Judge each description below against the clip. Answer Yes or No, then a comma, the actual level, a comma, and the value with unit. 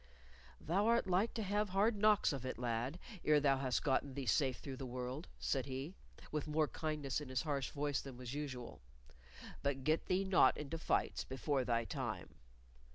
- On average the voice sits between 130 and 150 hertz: Yes, medium, 140 Hz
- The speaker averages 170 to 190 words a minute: Yes, average, 185 wpm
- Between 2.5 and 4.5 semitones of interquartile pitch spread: Yes, average, 3.8 semitones